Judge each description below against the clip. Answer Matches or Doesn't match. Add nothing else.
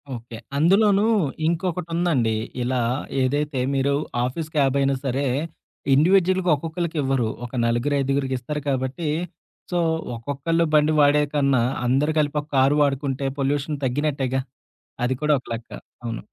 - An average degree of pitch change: Matches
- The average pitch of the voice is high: Doesn't match